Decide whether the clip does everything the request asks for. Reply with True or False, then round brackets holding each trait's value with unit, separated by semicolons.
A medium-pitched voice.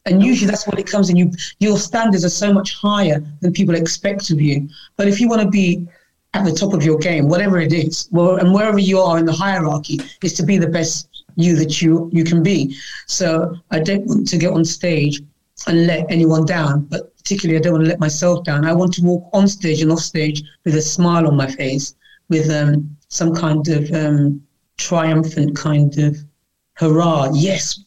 True (165 Hz)